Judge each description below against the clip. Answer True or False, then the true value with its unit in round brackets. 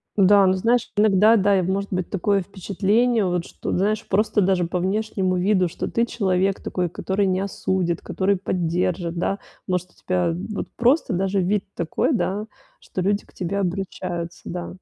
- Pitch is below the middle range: False (190 Hz)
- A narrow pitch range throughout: True (2.2 semitones)